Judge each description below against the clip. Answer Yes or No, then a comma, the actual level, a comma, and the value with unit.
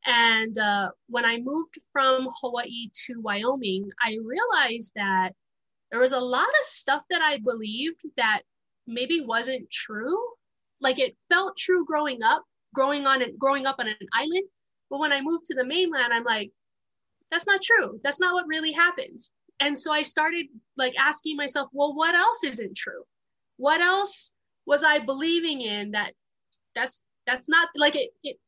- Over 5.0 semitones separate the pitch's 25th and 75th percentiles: Yes, wide, 5.4 semitones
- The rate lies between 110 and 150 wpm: No, average, 170 wpm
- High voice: Yes, very high, 280 Hz